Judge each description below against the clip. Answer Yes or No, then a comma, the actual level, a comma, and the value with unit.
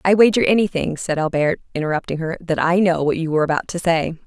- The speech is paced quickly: Yes, fast, 225 wpm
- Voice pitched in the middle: Yes, medium, 170 Hz